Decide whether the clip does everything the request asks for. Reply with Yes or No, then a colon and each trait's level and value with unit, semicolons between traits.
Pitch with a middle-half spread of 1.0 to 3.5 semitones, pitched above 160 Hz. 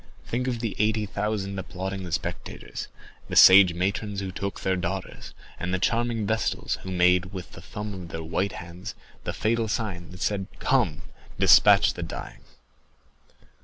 No: average, 2.8 semitones; very low, 95 Hz